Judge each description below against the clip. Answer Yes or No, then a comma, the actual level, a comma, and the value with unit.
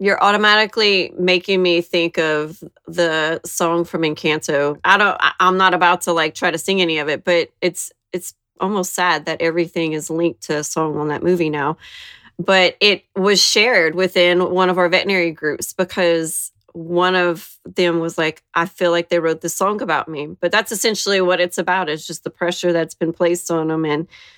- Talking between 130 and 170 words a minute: No, average, 195 wpm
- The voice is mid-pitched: Yes, medium, 175 Hz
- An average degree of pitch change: No, narrow, 2.1 semitones